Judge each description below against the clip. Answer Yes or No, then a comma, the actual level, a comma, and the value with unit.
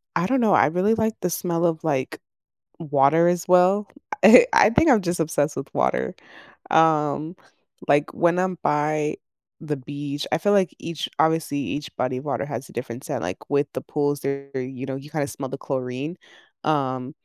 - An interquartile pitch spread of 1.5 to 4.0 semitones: Yes, average, 3.7 semitones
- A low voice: No, medium, 150 Hz